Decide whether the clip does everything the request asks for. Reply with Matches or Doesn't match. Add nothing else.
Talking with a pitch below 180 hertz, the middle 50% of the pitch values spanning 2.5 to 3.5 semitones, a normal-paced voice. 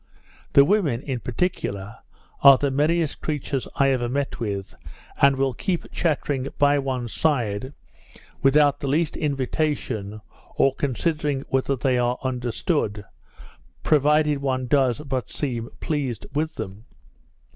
Doesn't match